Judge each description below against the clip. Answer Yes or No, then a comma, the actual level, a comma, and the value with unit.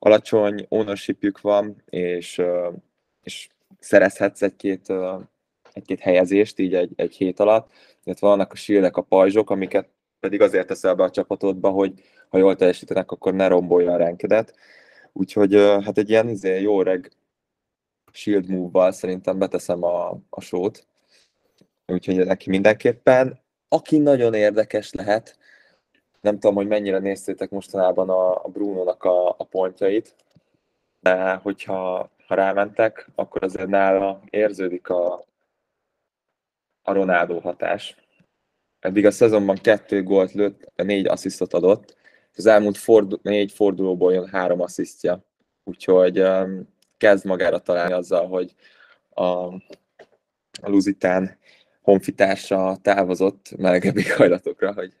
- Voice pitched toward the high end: No, very low, 95 Hz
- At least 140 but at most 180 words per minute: No, average, 120 wpm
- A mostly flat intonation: Yes, narrow, 1.8 semitones